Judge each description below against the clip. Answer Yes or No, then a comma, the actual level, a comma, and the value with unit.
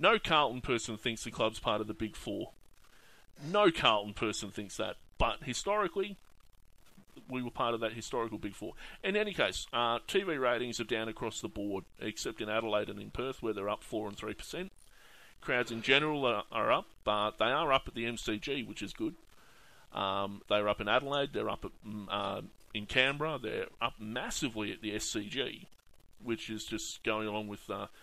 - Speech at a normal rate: Yes, average, 195 wpm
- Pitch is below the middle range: Yes, low, 110 Hz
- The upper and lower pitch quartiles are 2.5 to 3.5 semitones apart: Yes, average, 3.2 semitones